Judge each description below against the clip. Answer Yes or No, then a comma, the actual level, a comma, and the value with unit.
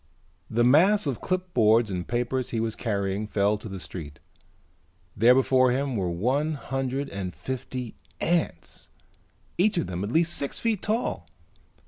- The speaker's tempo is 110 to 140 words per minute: No, average, 150 wpm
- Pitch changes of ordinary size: No, wide, 5.9 semitones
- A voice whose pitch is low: Yes, low, 125 Hz